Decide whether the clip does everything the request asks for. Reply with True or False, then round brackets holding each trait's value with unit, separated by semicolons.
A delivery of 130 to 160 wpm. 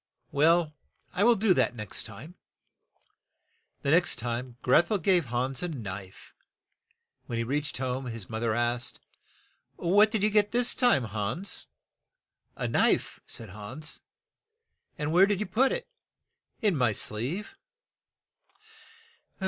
True (140 wpm)